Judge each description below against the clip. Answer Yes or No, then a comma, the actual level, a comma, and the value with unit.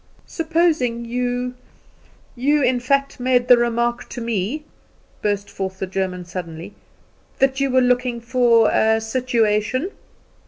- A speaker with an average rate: No, slow, 125 wpm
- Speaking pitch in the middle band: No, high, 240 Hz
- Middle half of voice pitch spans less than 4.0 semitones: Yes, average, 3.3 semitones